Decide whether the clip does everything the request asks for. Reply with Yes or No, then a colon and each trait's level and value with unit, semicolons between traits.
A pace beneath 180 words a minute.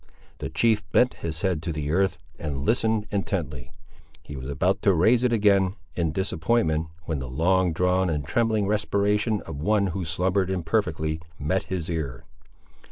Yes: average, 165 wpm